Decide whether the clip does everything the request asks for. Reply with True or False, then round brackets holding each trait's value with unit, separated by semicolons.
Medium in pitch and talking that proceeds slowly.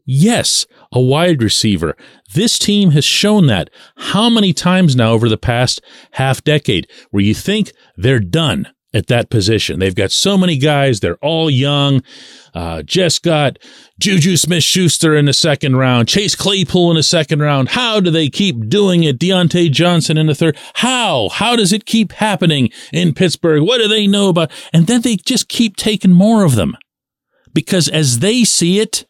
False (165 Hz; 180 wpm)